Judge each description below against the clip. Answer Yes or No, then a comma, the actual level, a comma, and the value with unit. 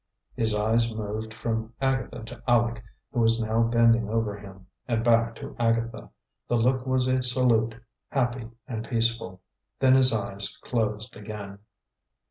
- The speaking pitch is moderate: No, low, 115 Hz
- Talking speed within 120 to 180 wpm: Yes, average, 145 wpm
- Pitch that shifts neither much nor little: No, narrow, 1.6 semitones